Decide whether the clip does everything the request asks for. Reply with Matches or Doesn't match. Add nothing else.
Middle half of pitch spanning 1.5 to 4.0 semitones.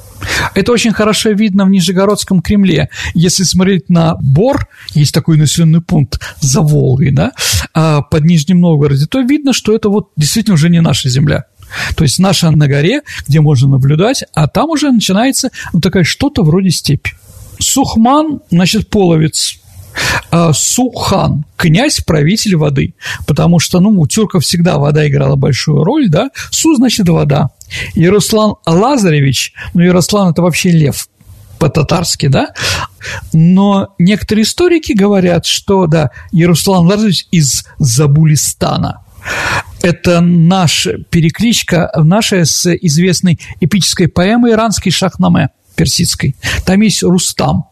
Doesn't match